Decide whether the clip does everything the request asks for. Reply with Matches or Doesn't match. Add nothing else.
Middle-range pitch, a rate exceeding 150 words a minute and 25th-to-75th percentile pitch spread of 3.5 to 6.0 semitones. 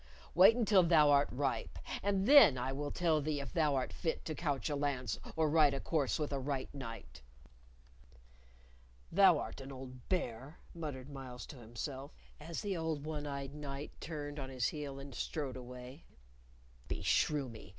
Doesn't match